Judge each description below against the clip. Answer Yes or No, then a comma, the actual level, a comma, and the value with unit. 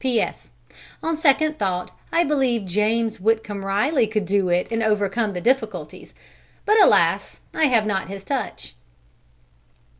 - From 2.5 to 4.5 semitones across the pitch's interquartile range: No, average, 5.2 semitones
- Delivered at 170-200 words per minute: No, average, 140 wpm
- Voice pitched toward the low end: No, high, 220 Hz